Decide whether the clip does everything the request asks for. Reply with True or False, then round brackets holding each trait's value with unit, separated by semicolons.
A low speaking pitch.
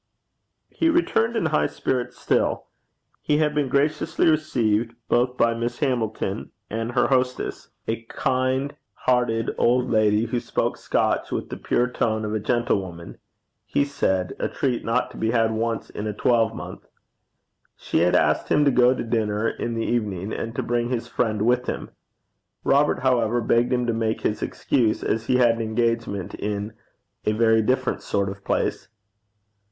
True (115 Hz)